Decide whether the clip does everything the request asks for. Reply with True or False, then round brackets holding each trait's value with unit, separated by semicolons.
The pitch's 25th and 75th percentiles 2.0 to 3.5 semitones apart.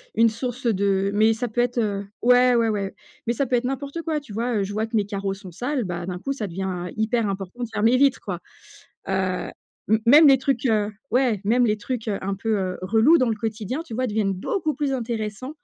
False (3.9 semitones)